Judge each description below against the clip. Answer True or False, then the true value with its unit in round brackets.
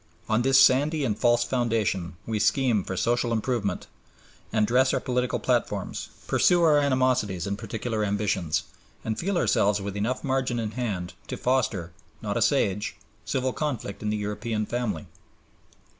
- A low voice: True (115 Hz)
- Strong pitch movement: False (3.9 semitones)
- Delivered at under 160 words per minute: True (150 wpm)